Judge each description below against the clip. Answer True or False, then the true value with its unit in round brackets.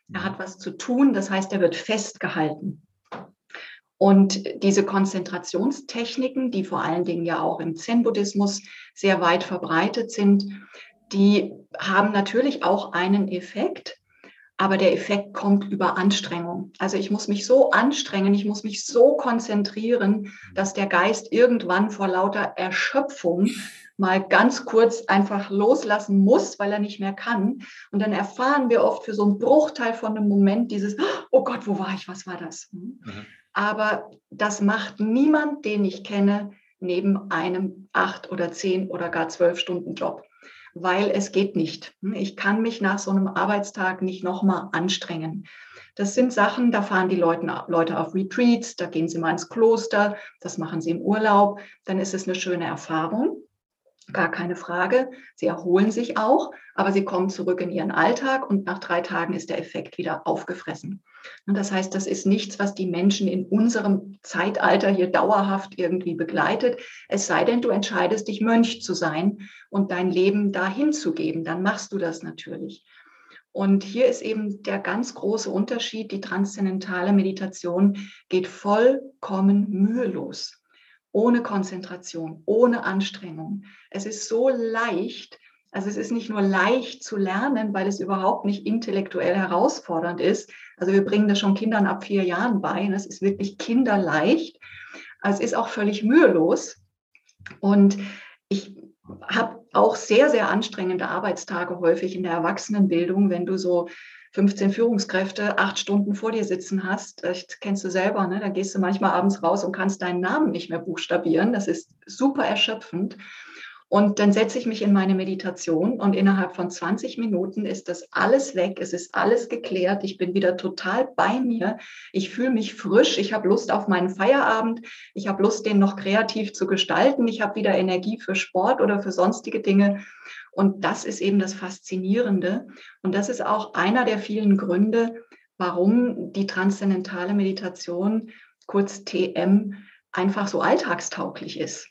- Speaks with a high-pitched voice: True (195 Hz)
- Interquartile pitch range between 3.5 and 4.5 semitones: False (2.7 semitones)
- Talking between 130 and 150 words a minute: False (165 wpm)